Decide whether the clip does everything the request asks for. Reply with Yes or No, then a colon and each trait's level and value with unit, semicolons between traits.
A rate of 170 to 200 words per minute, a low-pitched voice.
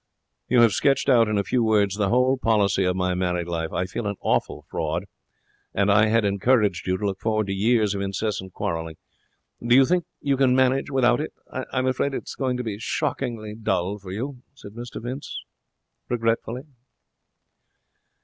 Yes: average, 180 wpm; low, 110 Hz